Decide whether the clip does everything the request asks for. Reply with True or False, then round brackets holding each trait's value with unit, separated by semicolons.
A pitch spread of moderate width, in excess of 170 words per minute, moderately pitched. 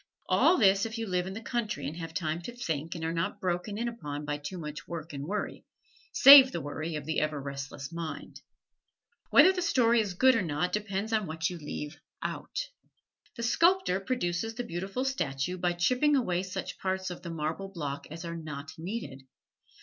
False (6.1 semitones; 195 wpm; 175 Hz)